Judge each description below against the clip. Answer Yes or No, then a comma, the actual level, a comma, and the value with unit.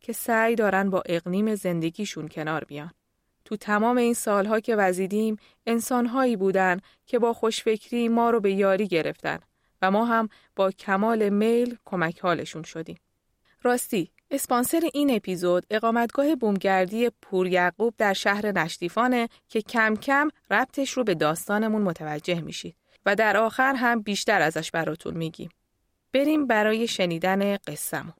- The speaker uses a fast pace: No, average, 135 wpm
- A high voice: Yes, high, 210 Hz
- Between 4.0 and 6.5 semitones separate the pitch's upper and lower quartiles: Yes, average, 4.3 semitones